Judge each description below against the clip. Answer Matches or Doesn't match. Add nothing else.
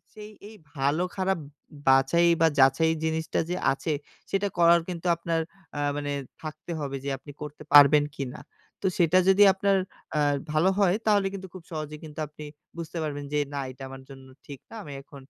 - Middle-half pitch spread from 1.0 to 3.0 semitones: Doesn't match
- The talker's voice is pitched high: Doesn't match